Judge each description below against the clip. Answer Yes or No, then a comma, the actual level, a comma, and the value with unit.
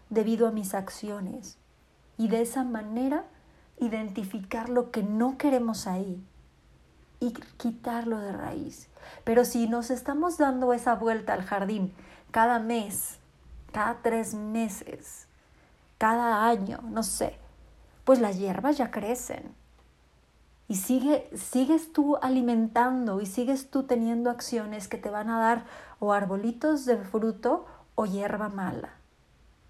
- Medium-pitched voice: No, high, 230 Hz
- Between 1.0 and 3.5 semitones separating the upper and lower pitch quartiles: Yes, average, 2.9 semitones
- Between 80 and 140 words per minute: Yes, slow, 125 wpm